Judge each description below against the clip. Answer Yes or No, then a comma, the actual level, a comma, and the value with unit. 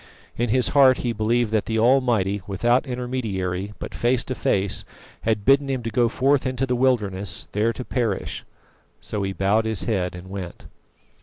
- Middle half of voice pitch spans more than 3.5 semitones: Yes, average, 4.0 semitones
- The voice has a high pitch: No, low, 115 Hz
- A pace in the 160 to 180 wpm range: Yes, average, 175 wpm